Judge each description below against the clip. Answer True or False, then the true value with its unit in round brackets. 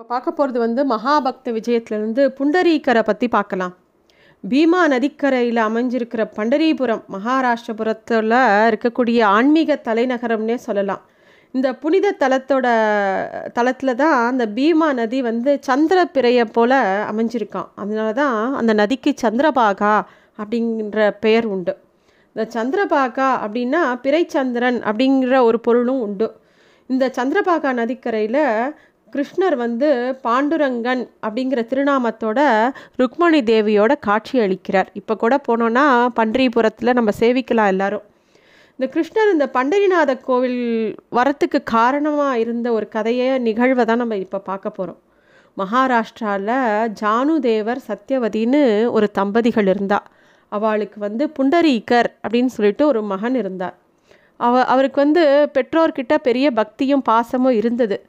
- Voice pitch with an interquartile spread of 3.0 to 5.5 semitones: True (3.8 semitones)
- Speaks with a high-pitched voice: True (240 Hz)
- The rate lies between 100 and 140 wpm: True (105 wpm)